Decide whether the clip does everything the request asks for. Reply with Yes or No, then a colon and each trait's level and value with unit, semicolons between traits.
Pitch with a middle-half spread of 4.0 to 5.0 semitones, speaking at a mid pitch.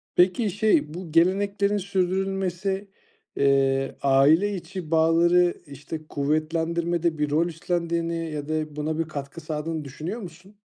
No: average, 3.2 semitones; medium, 165 Hz